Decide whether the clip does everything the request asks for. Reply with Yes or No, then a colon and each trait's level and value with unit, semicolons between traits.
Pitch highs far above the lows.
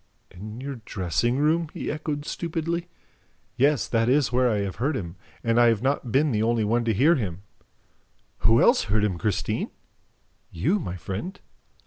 Yes: wide, 5.7 semitones